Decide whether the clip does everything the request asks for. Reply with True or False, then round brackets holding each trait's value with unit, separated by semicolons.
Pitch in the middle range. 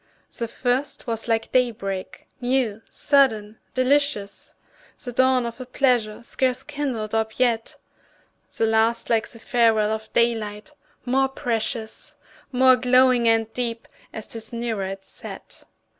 False (235 Hz)